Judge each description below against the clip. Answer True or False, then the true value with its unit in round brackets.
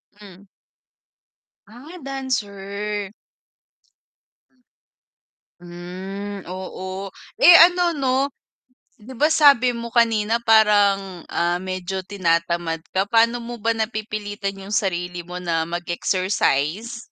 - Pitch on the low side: False (200 Hz)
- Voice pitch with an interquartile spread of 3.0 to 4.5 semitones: True (4.1 semitones)